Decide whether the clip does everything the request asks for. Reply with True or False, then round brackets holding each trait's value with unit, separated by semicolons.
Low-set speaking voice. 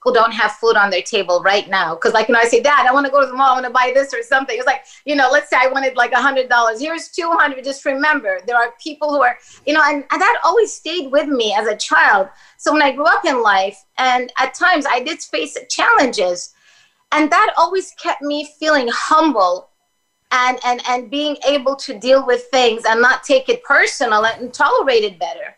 False (270 Hz)